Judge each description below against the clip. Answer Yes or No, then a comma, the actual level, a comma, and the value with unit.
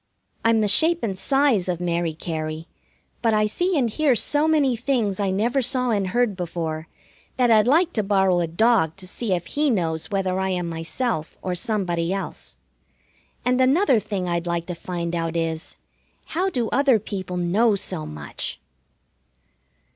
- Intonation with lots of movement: Yes, wide, 6.2 semitones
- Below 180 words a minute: Yes, average, 170 wpm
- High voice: Yes, high, 195 Hz